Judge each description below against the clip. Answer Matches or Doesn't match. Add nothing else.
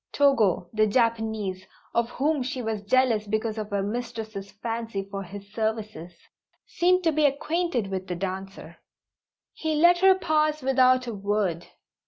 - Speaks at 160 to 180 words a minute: Doesn't match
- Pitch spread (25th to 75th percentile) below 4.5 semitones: Doesn't match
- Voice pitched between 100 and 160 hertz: Doesn't match